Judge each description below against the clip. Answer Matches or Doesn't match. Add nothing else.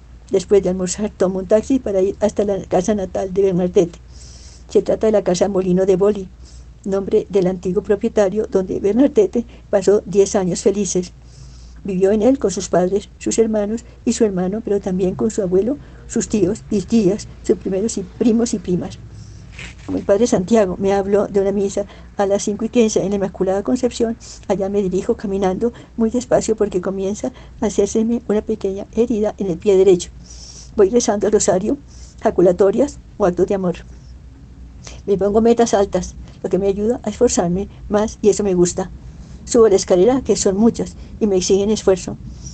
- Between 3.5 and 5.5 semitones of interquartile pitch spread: Doesn't match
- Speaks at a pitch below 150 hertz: Doesn't match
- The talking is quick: Doesn't match